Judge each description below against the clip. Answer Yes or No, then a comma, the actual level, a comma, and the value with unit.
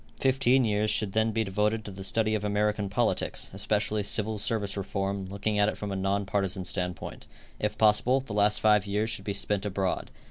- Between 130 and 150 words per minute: No, average, 200 wpm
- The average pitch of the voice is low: Yes, low, 105 Hz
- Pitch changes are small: Yes, narrow, 1.7 semitones